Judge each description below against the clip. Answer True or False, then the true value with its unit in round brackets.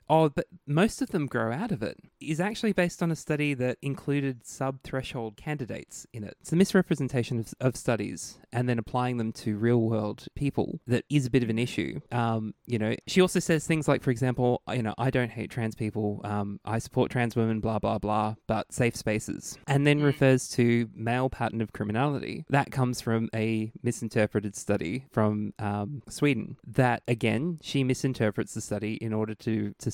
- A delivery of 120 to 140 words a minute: False (195 wpm)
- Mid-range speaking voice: False (120 Hz)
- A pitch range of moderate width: True (4.1 semitones)